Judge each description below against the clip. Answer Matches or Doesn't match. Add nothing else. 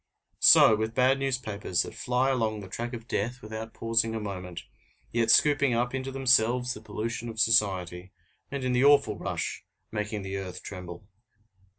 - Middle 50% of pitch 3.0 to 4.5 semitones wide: Matches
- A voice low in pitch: Matches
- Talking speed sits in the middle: Matches